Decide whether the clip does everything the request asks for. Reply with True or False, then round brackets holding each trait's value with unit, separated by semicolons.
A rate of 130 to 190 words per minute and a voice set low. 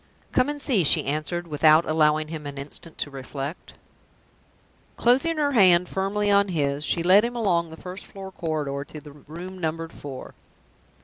False (170 wpm; 165 Hz)